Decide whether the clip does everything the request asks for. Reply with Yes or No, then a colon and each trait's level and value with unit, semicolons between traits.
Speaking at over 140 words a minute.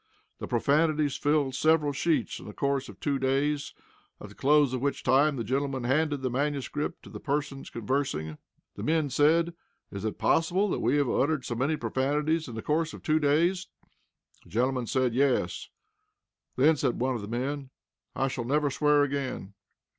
Yes: average, 180 wpm